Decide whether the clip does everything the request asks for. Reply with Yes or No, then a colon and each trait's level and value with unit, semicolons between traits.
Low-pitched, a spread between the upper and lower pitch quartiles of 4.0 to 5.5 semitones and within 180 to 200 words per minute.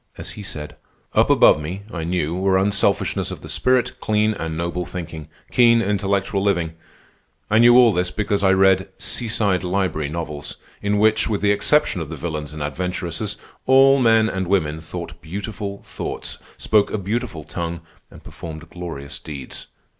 No: very low, 95 Hz; average, 4.3 semitones; average, 165 wpm